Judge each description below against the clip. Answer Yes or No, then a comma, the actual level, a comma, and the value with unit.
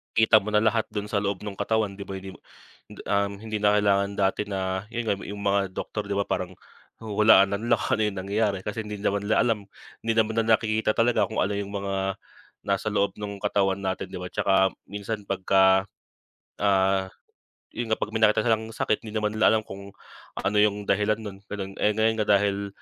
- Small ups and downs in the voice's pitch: Yes, narrow, 1.7 semitones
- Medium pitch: No, low, 100 Hz